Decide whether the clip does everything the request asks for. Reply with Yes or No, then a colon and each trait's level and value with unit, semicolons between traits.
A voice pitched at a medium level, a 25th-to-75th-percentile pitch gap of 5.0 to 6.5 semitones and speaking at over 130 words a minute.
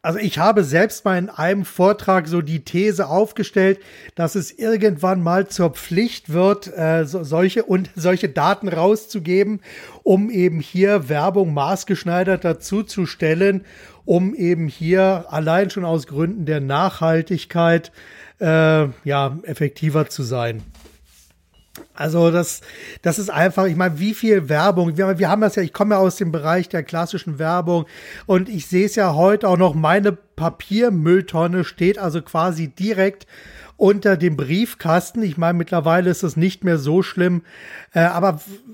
No: medium, 180 Hz; average, 3.2 semitones; average, 155 wpm